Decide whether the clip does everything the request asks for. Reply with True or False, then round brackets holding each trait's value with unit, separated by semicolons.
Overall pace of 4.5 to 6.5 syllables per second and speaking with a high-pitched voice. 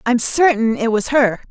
True (4.6 syllables/s; 240 Hz)